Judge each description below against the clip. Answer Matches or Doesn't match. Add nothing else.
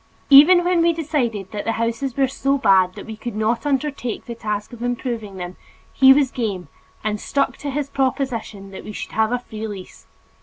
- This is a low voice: Doesn't match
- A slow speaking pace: Doesn't match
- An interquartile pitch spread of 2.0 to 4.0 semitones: Doesn't match